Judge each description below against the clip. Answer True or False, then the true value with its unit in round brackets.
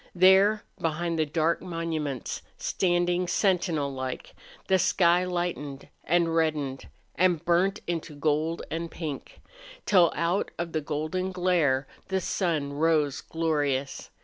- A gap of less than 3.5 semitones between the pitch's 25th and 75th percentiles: True (3.0 semitones)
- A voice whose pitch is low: False (165 Hz)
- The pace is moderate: False (120 wpm)